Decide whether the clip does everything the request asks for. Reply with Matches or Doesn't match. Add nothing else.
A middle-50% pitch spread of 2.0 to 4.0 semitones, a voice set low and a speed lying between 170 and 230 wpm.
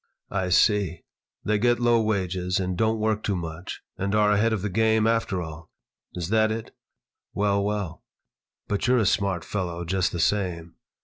Matches